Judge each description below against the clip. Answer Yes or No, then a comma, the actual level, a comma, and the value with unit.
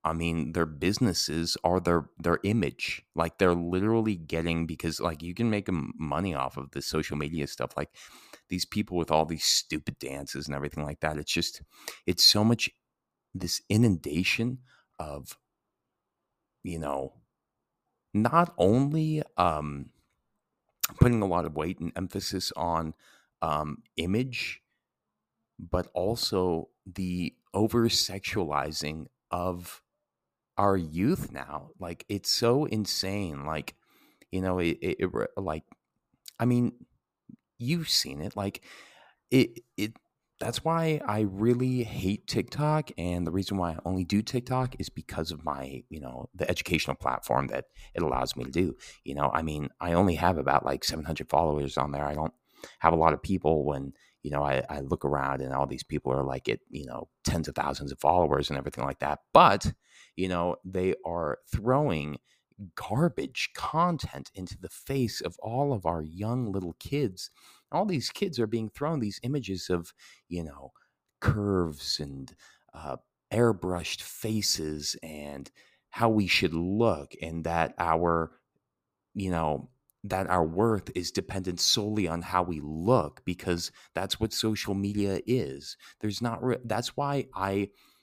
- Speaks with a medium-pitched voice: No, very low, 90 Hz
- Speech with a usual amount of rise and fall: No, wide, 5.7 semitones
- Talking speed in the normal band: Yes, average, 155 wpm